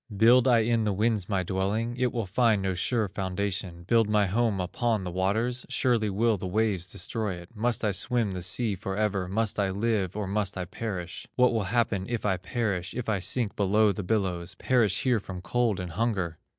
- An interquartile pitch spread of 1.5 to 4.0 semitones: Yes, average, 3.5 semitones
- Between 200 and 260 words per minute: Yes, fast, 205 wpm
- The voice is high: No, low, 105 Hz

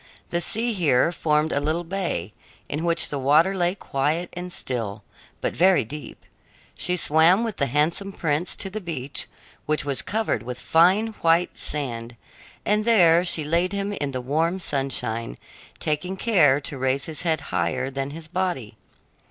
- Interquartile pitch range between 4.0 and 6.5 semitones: Yes, average, 4.8 semitones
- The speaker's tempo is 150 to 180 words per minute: Yes, average, 165 wpm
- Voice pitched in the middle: Yes, medium, 160 Hz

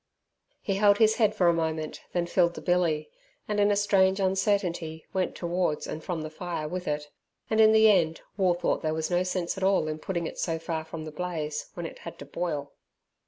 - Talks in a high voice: No, medium, 175 Hz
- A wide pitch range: No, average, 3.3 semitones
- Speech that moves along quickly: Yes, fast, 220 wpm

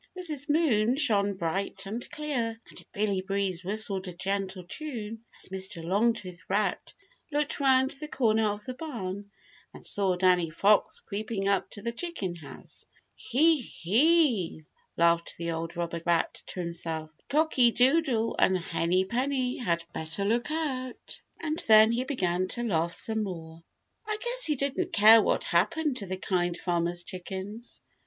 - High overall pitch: Yes, high, 210 Hz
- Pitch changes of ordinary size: No, wide, 5.9 semitones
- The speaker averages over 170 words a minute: No, average, 155 wpm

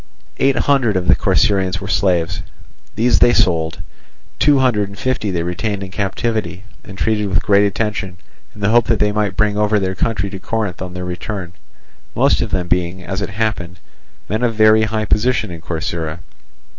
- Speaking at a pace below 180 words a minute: No, average, 185 wpm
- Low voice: Yes, low, 100 Hz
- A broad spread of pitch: No, average, 3.2 semitones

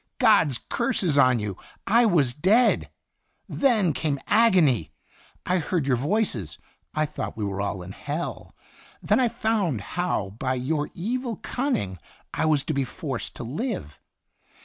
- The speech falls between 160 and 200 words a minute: No, average, 150 wpm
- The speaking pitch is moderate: Yes, medium, 155 Hz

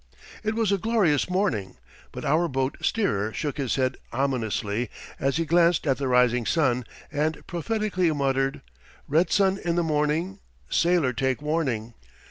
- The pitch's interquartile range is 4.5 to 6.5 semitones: Yes, average, 5.2 semitones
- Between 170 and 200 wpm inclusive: No, average, 150 wpm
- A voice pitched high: No, medium, 150 Hz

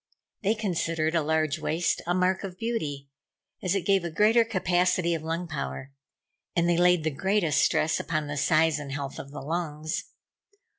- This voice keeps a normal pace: Yes, average, 180 wpm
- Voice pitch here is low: No, medium, 165 Hz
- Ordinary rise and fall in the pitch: Yes, average, 3.0 semitones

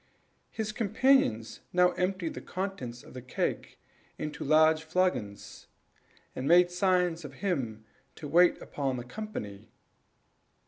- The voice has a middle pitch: Yes, medium, 165 Hz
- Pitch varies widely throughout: Yes, wide, 6.3 semitones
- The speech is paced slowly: Yes, slow, 125 wpm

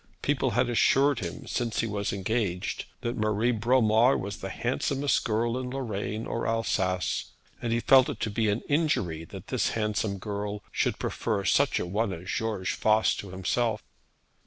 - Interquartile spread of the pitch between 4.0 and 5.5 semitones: No, average, 3.1 semitones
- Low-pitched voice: Yes, low, 110 Hz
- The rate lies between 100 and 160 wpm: No, average, 170 wpm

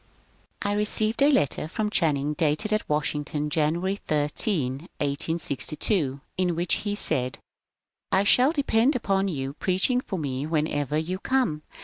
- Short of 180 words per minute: Yes, average, 140 wpm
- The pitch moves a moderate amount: No, wide, 5.8 semitones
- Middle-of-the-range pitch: Yes, medium, 165 Hz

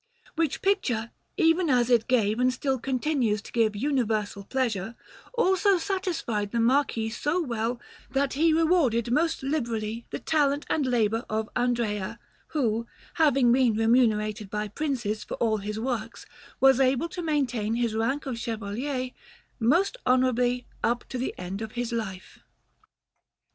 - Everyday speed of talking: Yes, average, 145 wpm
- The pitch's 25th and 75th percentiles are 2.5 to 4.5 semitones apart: Yes, average, 4.1 semitones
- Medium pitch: No, high, 245 Hz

